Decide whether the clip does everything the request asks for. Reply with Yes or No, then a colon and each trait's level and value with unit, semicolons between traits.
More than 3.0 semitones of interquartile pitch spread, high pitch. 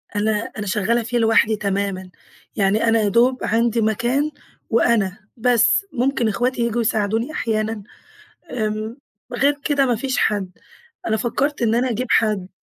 No: narrow, 2.4 semitones; high, 225 Hz